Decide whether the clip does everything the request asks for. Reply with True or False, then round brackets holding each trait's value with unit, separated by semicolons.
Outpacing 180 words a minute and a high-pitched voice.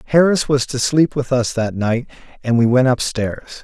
False (200 wpm; 130 Hz)